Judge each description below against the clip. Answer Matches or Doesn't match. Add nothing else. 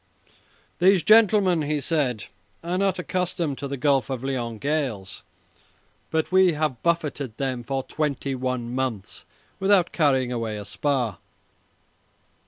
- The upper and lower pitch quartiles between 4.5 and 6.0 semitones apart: Matches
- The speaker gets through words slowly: Matches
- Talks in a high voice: Doesn't match